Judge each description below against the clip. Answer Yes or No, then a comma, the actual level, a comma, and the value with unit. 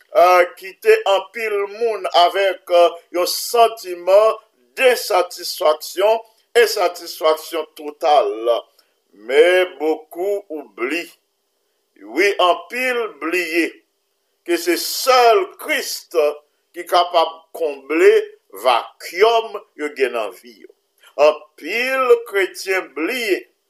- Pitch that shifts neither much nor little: No, wide, 7.1 semitones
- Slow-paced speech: Yes, slow, 85 wpm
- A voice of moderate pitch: No, high, 205 Hz